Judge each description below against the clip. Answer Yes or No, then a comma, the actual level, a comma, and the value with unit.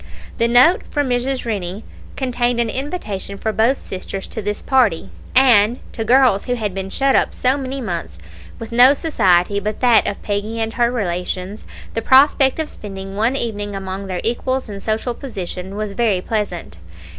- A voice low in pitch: No, high, 220 Hz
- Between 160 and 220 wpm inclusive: Yes, average, 175 wpm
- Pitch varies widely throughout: No, average, 4.3 semitones